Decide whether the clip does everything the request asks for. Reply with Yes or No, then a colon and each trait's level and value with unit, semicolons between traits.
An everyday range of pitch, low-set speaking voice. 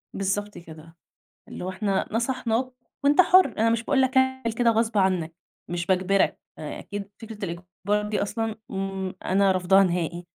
No: average, 3.5 semitones; high, 195 Hz